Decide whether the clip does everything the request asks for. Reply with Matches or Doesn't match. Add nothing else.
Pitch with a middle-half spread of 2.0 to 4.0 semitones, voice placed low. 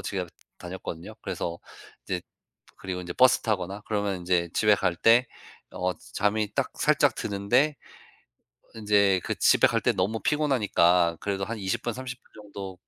Matches